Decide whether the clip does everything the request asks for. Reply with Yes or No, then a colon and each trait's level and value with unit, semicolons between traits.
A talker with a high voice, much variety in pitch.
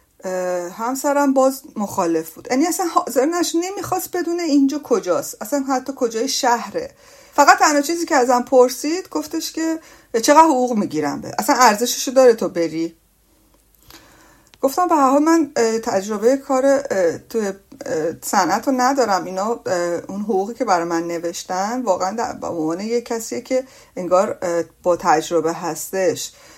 Yes: very high, 250 Hz; wide, 7.4 semitones